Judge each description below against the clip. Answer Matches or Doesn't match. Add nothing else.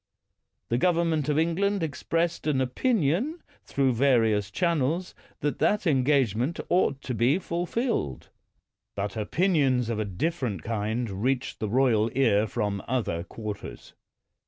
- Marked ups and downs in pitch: Matches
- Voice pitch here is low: Matches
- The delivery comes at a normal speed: Doesn't match